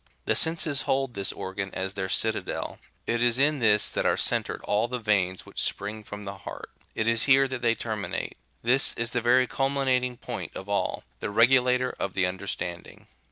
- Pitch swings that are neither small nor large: Yes, average, 4.1 semitones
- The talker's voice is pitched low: Yes, low, 115 Hz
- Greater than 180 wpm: Yes, average, 190 wpm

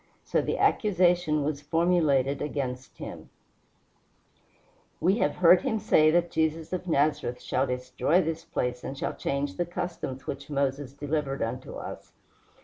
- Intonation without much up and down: No, average, 3.9 semitones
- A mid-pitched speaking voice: Yes, medium, 150 Hz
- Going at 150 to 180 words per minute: No, average, 140 wpm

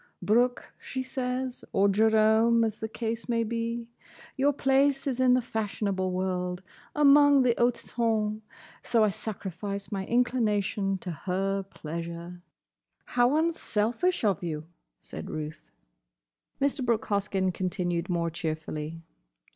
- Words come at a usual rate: No, slow, 120 wpm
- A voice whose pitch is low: No, high, 215 Hz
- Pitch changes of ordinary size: Yes, average, 4.7 semitones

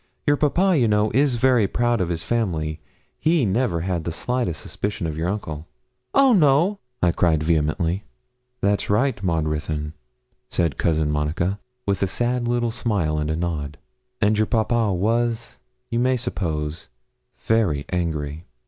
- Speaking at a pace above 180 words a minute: No, average, 155 wpm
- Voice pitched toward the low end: Yes, low, 100 Hz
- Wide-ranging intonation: Yes, wide, 6.9 semitones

